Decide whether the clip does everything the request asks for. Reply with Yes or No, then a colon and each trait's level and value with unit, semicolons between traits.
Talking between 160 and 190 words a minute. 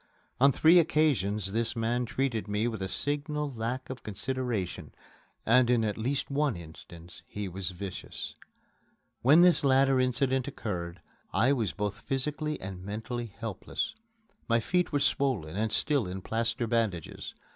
No: average, 145 wpm